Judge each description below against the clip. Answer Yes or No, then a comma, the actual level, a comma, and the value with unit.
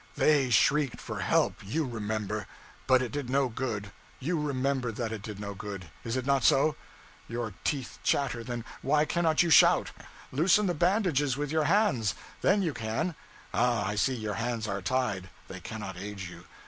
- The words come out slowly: No, average, 180 wpm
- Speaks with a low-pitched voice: Yes, low, 125 Hz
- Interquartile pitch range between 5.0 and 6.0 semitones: Yes, wide, 5.5 semitones